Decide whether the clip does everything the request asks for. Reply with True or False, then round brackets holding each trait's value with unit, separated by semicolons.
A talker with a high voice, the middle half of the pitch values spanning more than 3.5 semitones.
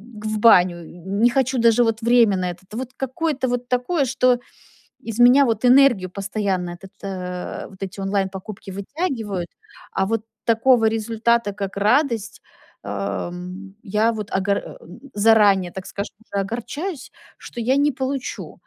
True (220 Hz; 4.1 semitones)